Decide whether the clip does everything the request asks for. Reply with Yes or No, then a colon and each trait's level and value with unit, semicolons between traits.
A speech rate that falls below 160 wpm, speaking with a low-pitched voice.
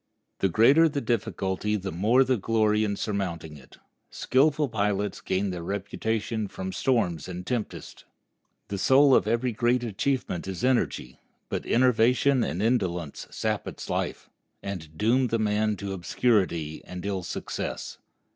Yes: average, 145 wpm; low, 105 Hz